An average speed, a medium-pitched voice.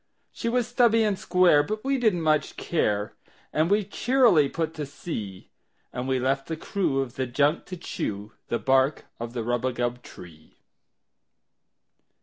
Yes: average, 155 wpm; medium, 145 Hz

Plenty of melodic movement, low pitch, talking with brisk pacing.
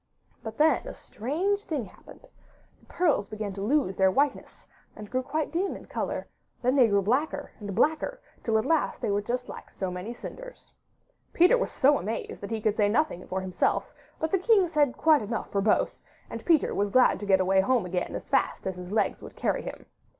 No: wide, 7.4 semitones; high, 235 Hz; fast, 210 wpm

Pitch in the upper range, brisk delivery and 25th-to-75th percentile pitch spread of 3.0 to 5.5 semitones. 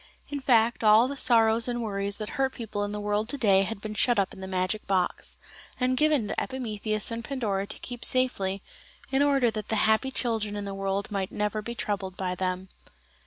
Yes: high, 215 Hz; fast, 215 wpm; average, 3.4 semitones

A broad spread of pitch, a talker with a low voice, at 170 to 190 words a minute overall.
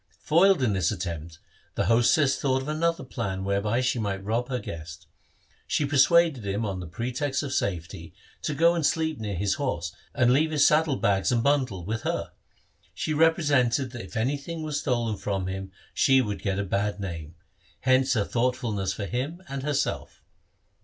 Yes: wide, 6.3 semitones; low, 120 Hz; average, 180 wpm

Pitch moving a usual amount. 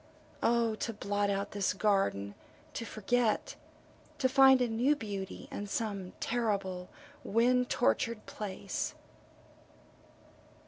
Yes: average, 3.2 semitones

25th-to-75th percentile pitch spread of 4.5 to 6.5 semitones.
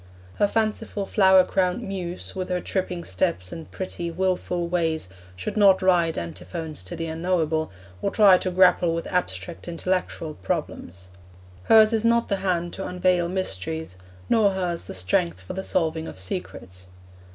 No: average, 2.9 semitones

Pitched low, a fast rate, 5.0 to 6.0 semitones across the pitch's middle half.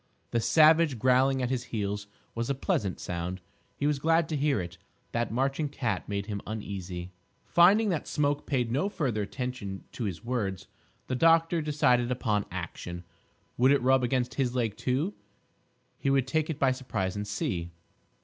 No: low, 125 Hz; average, 170 wpm; wide, 5.6 semitones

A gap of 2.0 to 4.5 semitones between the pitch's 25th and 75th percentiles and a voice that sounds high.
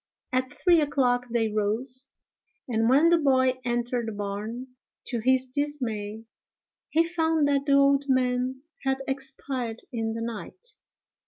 Yes: average, 3.2 semitones; very high, 255 Hz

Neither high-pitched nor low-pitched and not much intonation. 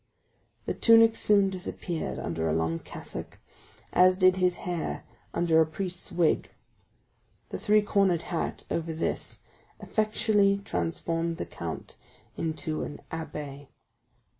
No: medium, 175 Hz; average, 3.6 semitones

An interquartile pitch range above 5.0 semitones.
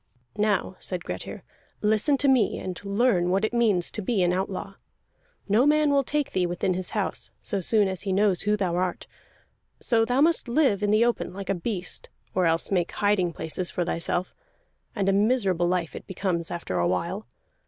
No: average, 3.6 semitones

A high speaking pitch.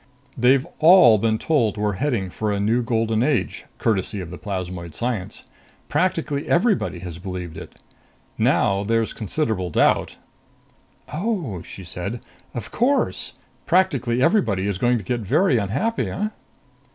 No: low, 115 Hz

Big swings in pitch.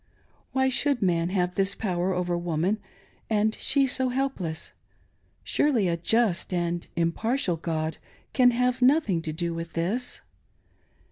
Yes: wide, 6.6 semitones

